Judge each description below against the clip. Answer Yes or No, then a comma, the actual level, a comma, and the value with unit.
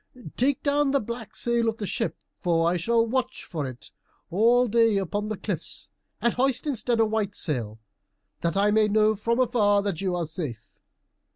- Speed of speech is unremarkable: Yes, average, 185 wpm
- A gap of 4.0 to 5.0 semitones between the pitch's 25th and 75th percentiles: Yes, average, 4.7 semitones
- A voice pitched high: Yes, high, 215 Hz